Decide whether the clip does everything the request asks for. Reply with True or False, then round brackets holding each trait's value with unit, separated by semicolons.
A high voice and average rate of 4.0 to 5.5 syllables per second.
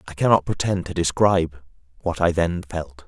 False (85 Hz; 5.2 syllables/s)